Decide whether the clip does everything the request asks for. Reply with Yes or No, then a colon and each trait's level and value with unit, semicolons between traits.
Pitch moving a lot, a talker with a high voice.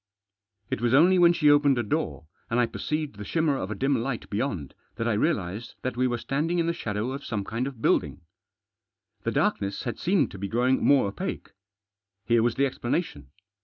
No: wide, 5.7 semitones; low, 120 Hz